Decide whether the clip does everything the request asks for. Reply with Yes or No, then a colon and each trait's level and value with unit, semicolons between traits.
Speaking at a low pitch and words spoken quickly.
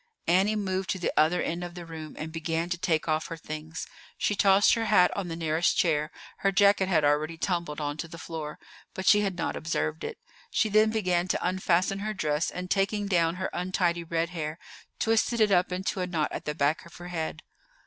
No: medium, 175 Hz; fast, 220 wpm